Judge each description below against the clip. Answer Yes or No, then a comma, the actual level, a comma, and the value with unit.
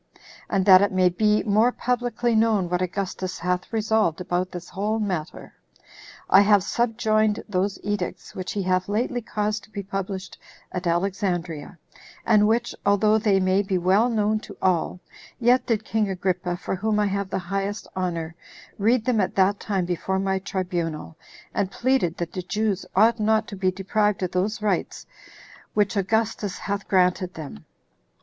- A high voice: Yes, high, 195 Hz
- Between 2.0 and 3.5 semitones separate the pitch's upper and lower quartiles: Yes, average, 2.8 semitones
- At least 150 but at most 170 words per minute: Yes, average, 165 wpm